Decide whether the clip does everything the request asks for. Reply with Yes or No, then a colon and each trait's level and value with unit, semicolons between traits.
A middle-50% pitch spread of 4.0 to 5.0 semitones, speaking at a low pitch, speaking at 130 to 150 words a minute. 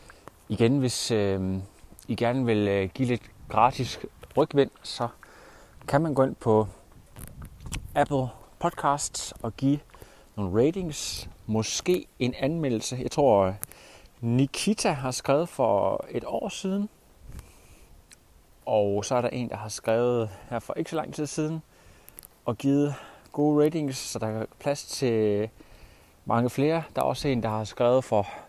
Yes: average, 4.7 semitones; low, 125 Hz; slow, 145 wpm